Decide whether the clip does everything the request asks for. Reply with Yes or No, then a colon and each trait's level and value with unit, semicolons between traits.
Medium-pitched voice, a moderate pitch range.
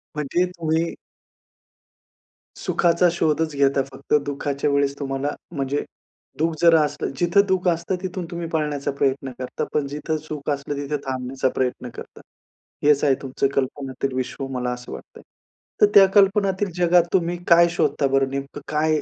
Yes: medium, 150 Hz; average, 3.7 semitones